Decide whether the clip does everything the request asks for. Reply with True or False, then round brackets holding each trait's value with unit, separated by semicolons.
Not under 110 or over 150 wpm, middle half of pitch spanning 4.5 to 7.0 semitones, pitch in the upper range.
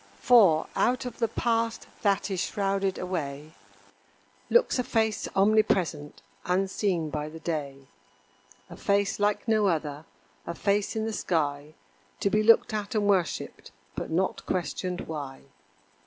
True (140 wpm; 5.1 semitones; 195 Hz)